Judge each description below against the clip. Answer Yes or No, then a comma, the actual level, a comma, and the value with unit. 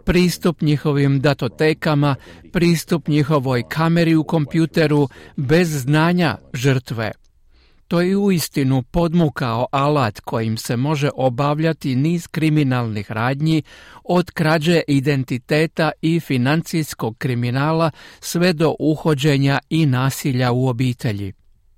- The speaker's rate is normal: No, slow, 100 wpm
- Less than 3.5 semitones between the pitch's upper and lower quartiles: No, average, 4.0 semitones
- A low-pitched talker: No, medium, 150 Hz